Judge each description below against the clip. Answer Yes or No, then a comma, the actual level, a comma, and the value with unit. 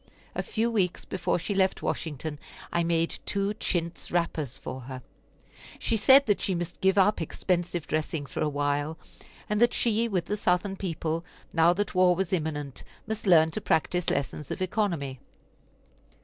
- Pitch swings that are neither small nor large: Yes, average, 4.0 semitones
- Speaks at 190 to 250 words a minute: No, average, 165 wpm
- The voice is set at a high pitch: No, medium, 175 Hz